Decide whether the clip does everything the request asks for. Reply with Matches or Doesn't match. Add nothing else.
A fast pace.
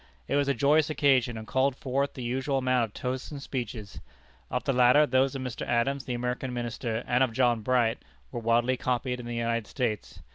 Matches